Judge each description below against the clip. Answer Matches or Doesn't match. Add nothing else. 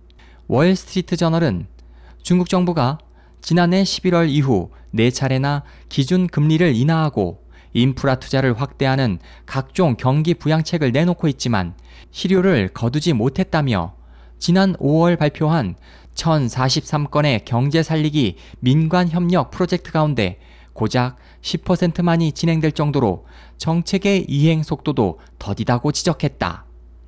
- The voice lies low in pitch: Doesn't match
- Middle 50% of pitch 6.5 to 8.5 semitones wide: Matches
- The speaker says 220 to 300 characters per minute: Matches